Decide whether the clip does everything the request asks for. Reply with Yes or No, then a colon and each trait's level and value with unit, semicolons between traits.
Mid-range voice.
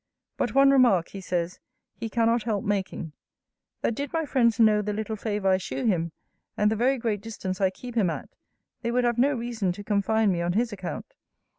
No: high, 215 Hz